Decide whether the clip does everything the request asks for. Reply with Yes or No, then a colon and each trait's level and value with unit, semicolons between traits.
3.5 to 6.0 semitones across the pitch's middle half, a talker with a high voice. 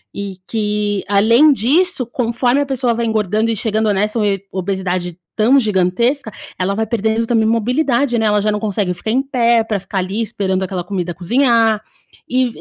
No: average, 3.1 semitones; high, 220 Hz